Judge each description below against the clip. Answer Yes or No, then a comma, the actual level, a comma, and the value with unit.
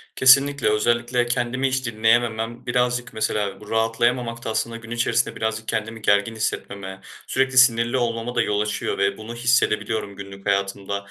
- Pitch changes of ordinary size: No, narrow, 2.3 semitones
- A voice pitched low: Yes, low, 115 Hz